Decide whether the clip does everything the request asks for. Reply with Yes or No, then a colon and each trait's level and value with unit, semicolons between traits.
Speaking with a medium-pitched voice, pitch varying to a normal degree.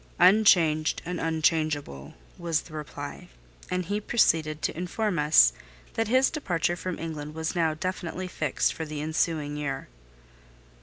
Yes: medium, 160 Hz; average, 3.0 semitones